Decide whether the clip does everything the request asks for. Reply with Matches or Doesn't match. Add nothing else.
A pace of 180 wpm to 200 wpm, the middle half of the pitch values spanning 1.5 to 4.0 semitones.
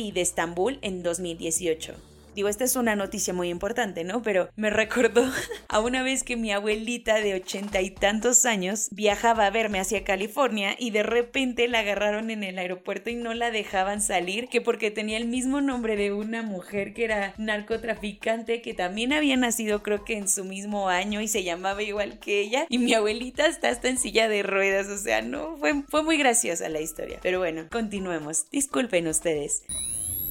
Matches